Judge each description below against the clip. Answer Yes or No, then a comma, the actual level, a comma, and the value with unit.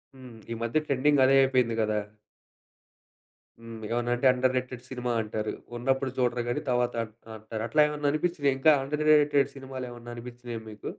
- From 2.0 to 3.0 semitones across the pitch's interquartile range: Yes, narrow, 2.4 semitones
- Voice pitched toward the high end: No, low, 125 Hz